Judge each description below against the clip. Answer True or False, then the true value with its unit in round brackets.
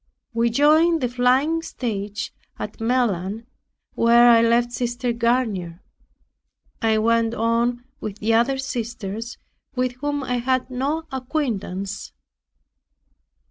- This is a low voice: False (240 Hz)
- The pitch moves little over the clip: True (2.3 semitones)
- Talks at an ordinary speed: False (110 wpm)